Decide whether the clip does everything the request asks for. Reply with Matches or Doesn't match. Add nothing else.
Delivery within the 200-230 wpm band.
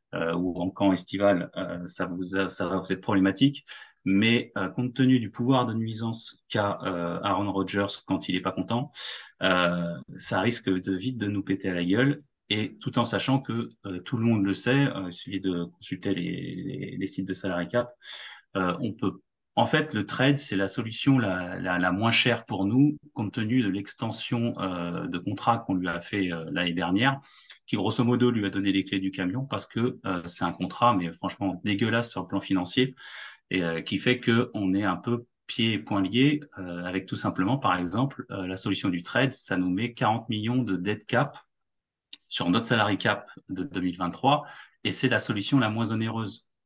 Matches